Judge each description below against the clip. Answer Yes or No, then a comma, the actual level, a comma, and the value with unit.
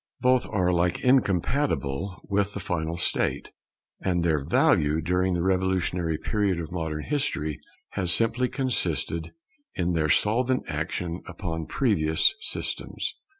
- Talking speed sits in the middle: No, slow, 125 wpm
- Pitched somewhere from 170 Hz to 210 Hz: No, very low, 90 Hz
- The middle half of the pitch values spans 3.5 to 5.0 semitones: Yes, average, 4.2 semitones